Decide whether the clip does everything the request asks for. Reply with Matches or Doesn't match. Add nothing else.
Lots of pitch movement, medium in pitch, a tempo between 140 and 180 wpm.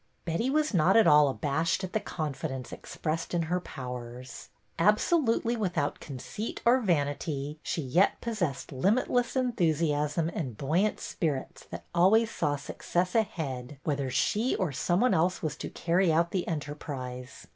Matches